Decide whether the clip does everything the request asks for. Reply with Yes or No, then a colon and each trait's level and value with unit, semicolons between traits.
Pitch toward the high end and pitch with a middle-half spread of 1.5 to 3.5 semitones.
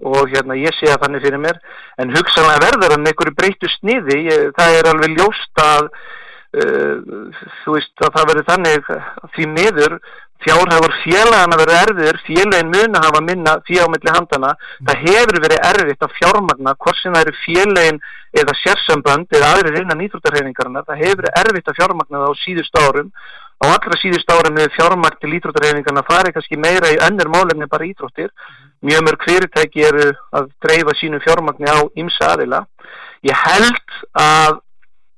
No: medium, 155 Hz; narrow, 2.6 semitones